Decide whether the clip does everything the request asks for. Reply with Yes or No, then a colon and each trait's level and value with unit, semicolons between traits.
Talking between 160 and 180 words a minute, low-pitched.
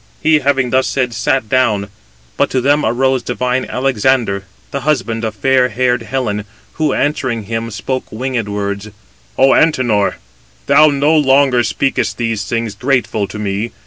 No: average, 150 wpm; low, 125 Hz